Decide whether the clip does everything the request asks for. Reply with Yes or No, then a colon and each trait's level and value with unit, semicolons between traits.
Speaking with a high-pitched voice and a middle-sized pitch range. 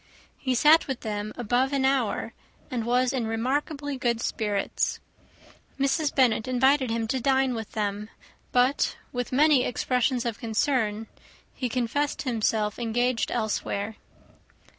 Yes: high, 245 Hz; average, 3.1 semitones